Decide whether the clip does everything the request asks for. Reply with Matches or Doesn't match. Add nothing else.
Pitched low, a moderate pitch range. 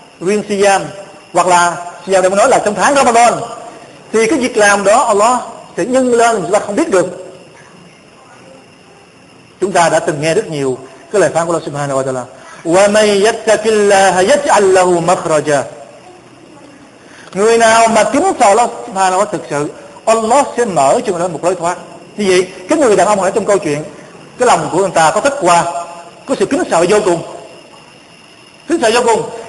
Doesn't match